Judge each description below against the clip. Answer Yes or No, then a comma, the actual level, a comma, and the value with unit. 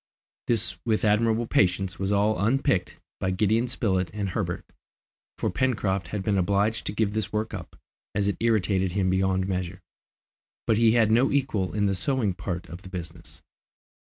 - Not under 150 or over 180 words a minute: Yes, average, 170 wpm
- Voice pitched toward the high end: No, low, 100 Hz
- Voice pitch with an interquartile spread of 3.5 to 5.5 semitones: No, average, 3.0 semitones